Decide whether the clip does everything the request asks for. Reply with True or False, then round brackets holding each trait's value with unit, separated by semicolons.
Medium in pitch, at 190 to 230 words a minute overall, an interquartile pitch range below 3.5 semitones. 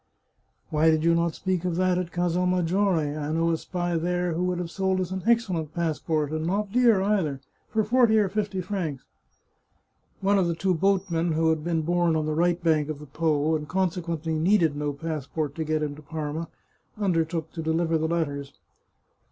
True (165 Hz; 200 wpm; 2.8 semitones)